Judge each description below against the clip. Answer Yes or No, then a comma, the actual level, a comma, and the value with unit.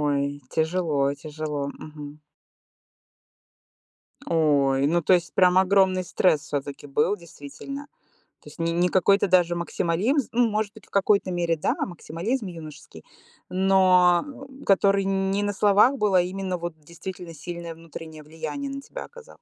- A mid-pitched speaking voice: Yes, medium, 180 Hz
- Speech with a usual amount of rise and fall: Yes, average, 3.8 semitones